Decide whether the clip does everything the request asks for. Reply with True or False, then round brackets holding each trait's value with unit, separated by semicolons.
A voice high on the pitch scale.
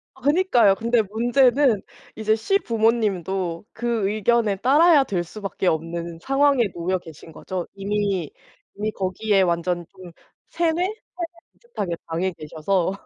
True (205 Hz)